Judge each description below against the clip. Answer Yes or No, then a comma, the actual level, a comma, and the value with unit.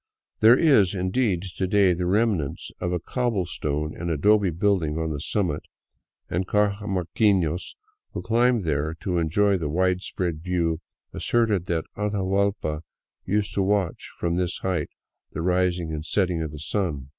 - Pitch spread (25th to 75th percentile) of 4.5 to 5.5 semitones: No, average, 3.8 semitones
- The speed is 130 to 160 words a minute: Yes, average, 150 wpm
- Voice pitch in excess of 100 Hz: No, very low, 90 Hz